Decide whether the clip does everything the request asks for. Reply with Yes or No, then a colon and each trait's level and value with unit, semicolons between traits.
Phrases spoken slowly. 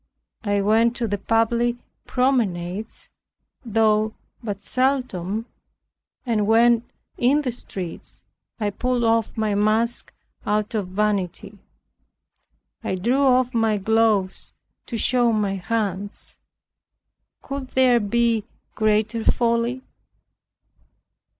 Yes: slow, 100 wpm